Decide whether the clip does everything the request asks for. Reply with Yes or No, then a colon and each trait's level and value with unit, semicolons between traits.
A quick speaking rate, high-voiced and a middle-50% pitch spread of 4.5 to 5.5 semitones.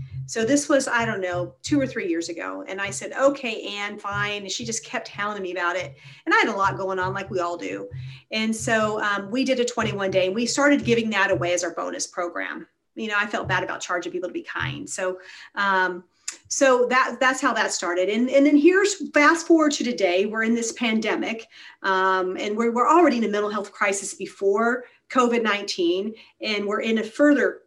Yes: fast, 225 wpm; high, 210 Hz; average, 5.2 semitones